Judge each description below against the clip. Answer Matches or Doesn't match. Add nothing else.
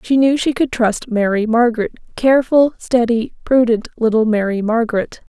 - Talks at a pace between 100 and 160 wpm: Matches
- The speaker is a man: Doesn't match